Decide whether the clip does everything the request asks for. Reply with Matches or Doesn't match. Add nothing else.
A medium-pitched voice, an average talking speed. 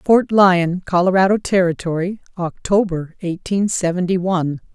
Doesn't match